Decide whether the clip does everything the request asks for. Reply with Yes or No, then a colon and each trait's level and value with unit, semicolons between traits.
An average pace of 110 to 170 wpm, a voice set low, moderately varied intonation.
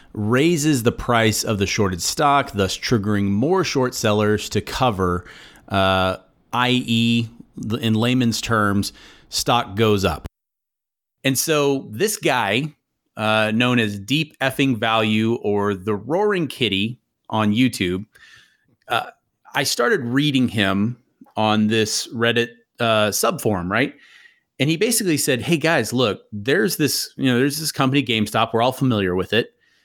Yes: average, 140 wpm; low, 115 Hz; average, 4.0 semitones